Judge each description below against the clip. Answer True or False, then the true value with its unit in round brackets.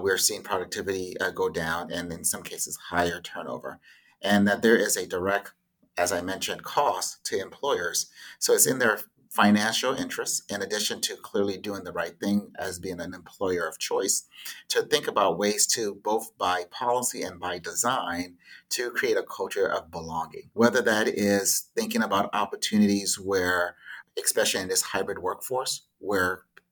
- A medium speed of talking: True (165 wpm)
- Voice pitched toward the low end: True (115 Hz)